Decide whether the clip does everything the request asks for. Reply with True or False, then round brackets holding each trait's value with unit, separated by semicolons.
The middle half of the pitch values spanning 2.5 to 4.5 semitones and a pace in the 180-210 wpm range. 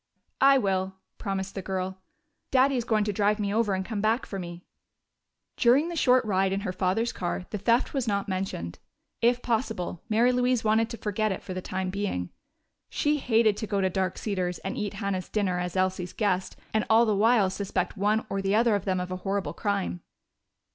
True (3.2 semitones; 205 wpm)